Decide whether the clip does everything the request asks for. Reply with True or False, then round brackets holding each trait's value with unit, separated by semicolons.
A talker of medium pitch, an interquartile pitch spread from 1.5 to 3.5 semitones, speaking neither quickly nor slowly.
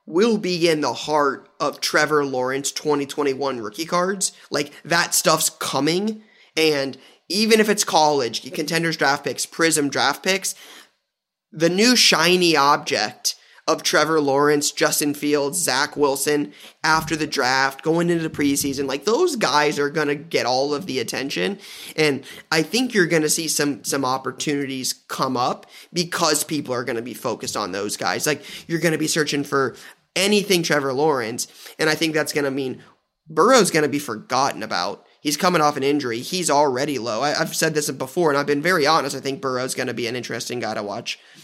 True (150 Hz; 3.0 semitones; 175 wpm)